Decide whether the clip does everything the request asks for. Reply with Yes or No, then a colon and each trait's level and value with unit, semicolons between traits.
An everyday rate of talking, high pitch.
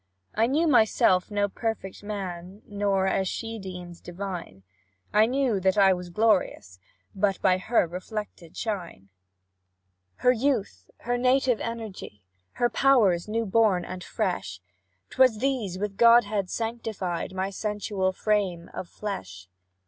No: slow, 130 wpm; high, 200 Hz